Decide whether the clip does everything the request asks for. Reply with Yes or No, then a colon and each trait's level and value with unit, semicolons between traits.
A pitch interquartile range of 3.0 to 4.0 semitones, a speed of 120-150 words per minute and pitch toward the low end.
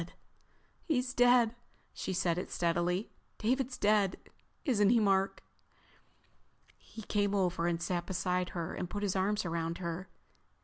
No: average, 3.4 semitones; slow, 135 wpm; high, 190 Hz